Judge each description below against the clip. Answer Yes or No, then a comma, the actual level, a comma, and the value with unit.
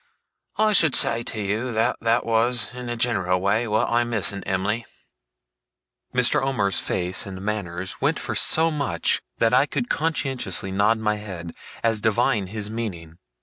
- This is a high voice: No, low, 110 Hz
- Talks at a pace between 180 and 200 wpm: No, average, 165 wpm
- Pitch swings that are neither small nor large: Yes, average, 3.8 semitones